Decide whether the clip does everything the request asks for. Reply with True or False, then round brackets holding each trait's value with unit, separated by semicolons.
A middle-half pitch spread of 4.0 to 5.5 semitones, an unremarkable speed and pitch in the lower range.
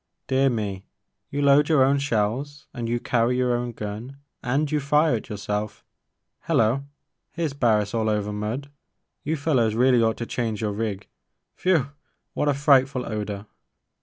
True (4.6 semitones; 170 wpm; 120 Hz)